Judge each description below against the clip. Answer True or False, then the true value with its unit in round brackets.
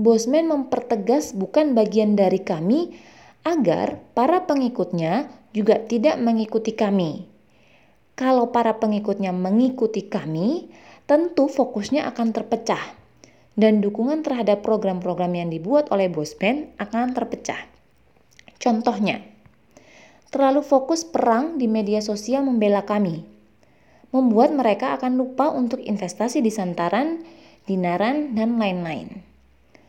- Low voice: False (225 Hz)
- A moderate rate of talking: True (105 wpm)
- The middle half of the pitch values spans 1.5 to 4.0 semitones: False (4.5 semitones)